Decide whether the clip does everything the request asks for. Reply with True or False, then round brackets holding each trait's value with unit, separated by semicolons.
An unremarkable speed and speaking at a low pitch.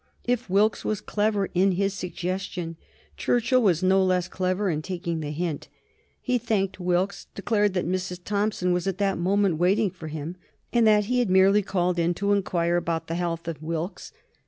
False (180 wpm; 185 Hz)